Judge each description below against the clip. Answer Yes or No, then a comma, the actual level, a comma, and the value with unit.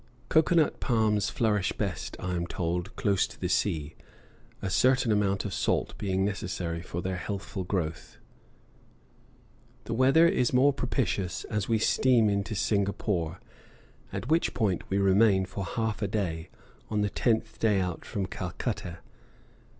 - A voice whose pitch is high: No, low, 100 Hz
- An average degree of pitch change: Yes, average, 3.6 semitones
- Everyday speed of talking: Yes, average, 150 wpm